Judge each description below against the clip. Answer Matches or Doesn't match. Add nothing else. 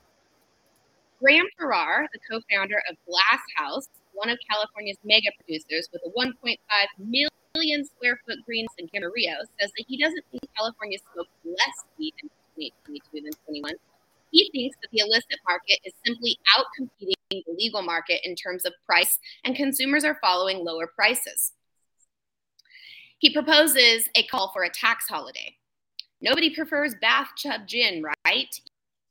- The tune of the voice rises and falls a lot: Matches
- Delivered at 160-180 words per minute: Doesn't match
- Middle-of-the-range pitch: Doesn't match